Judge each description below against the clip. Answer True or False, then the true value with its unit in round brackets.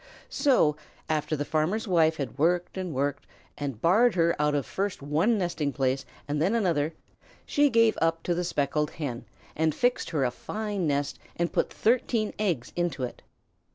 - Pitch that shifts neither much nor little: True (4.9 semitones)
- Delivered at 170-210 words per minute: True (175 wpm)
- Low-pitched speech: False (165 Hz)